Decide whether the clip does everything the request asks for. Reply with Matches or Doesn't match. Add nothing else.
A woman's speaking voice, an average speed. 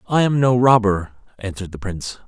Doesn't match